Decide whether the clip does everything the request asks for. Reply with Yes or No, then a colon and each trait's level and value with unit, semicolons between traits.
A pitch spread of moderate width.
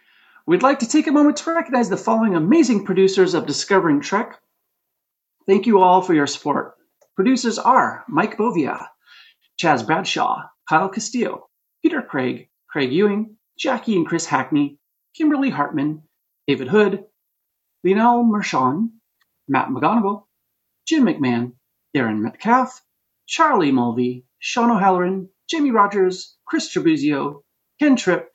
No: wide, 6.4 semitones